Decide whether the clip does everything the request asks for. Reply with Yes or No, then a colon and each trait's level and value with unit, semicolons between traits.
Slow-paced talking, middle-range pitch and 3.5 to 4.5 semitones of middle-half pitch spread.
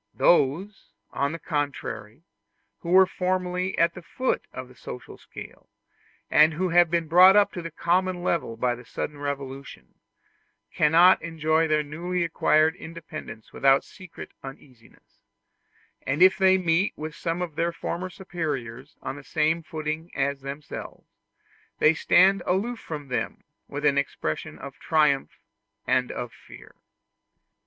No: average, 145 wpm; medium, 160 Hz; average, 4.0 semitones